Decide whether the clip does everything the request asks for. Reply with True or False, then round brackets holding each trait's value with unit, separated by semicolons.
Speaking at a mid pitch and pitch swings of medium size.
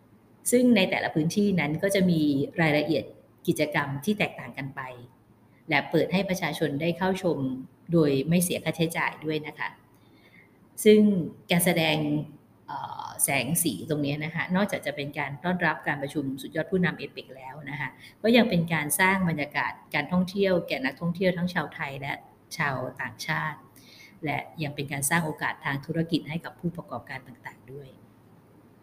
True (155 Hz; 4.1 semitones)